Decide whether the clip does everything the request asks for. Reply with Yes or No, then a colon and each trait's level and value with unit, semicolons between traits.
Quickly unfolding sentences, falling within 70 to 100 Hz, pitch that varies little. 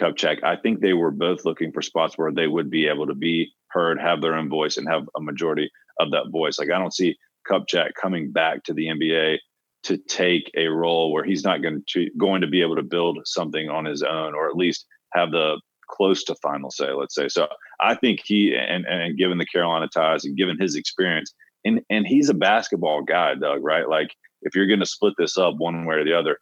Yes: fast, 235 wpm; very low, 85 Hz; narrow, 2.3 semitones